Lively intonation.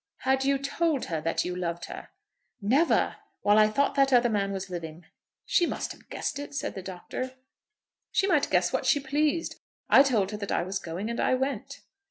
Yes: wide, 6.5 semitones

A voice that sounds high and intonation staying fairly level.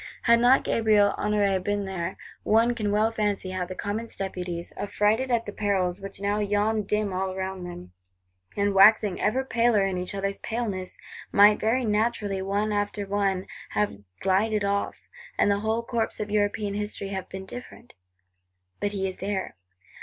Yes: high, 205 Hz; narrow, 2.0 semitones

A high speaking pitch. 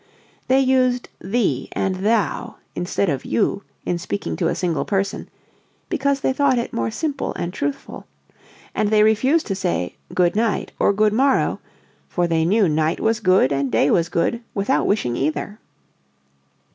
Yes: high, 200 Hz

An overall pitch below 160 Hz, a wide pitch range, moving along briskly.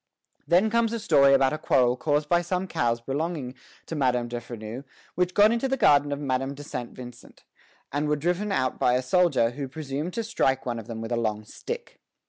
Yes: medium, 140 Hz; wide, 6.0 semitones; fast, 215 wpm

